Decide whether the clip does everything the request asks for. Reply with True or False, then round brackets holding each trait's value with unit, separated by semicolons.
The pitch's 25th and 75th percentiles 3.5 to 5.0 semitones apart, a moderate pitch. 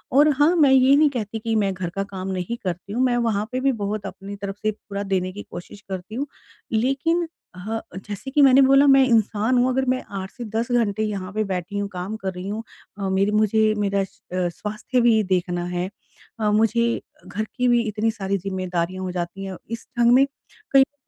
False (4.2 semitones; 215 Hz)